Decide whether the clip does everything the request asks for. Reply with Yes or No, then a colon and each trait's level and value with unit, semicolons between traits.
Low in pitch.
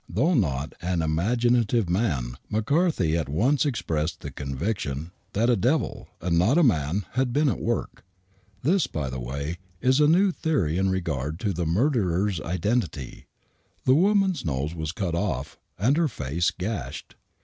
Yes: very low, 95 Hz